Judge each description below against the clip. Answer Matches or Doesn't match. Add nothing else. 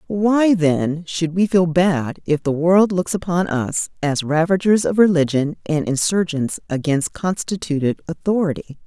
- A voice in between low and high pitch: Matches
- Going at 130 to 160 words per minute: Matches